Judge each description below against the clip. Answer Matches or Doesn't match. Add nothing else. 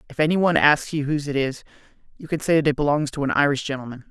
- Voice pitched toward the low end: Doesn't match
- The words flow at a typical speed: Doesn't match